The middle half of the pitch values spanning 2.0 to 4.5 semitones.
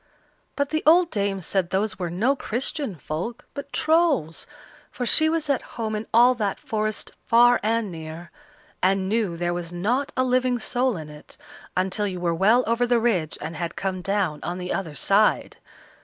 No: wide, 5.6 semitones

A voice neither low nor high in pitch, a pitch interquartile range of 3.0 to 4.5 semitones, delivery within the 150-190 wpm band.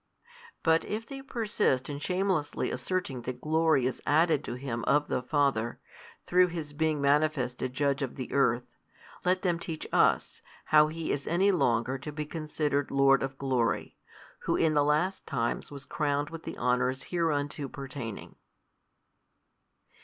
Yes: medium, 145 Hz; average, 3.6 semitones; average, 155 wpm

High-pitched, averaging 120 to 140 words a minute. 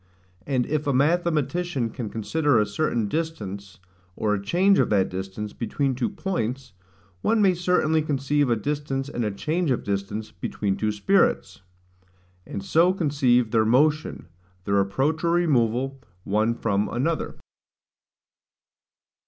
No: low, 130 Hz; slow, 135 wpm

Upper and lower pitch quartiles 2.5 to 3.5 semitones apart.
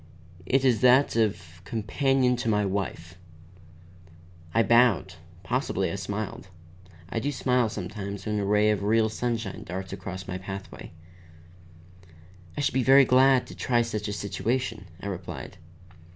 No: average, 4.2 semitones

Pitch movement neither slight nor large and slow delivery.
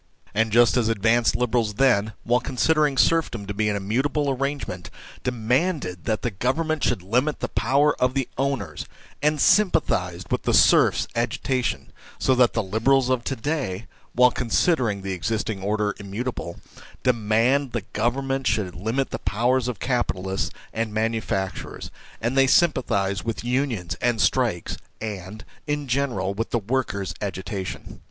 No: average, 4.5 semitones; average, 150 wpm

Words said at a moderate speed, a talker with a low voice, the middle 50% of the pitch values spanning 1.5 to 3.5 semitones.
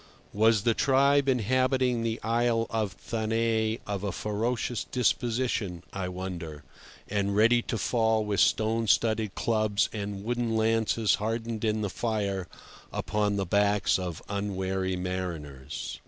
No: slow, 130 wpm; low, 110 Hz; average, 2.7 semitones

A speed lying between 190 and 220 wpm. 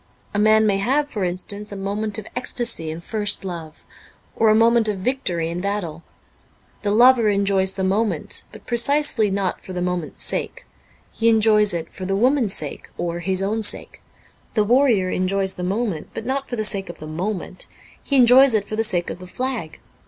Yes: average, 195 wpm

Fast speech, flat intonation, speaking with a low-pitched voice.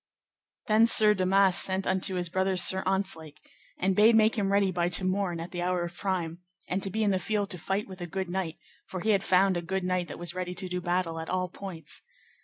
No: fast, 240 wpm; narrow, 1.8 semitones; medium, 185 Hz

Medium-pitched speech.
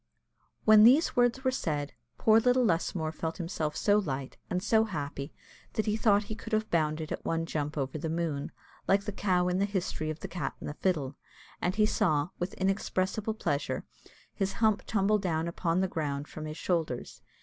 Yes: medium, 180 Hz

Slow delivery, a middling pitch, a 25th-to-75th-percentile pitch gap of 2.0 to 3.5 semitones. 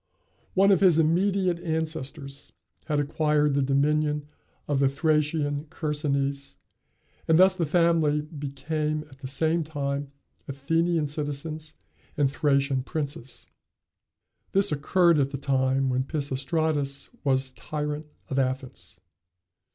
Yes: slow, 115 wpm; medium, 150 Hz; narrow, 2.5 semitones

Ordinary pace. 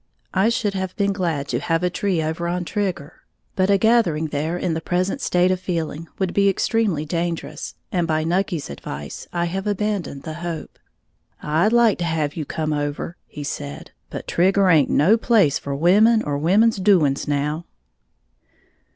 Yes: average, 175 wpm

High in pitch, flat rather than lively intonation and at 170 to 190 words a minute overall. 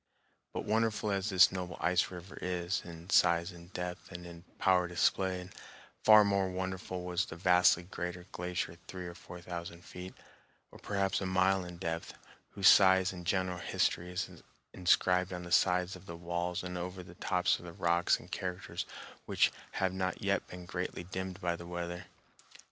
No: very low, 90 Hz; narrow, 1.2 semitones; average, 175 wpm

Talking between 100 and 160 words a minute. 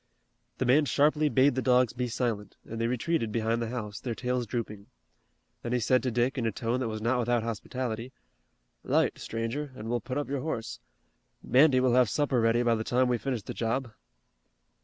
No: average, 200 wpm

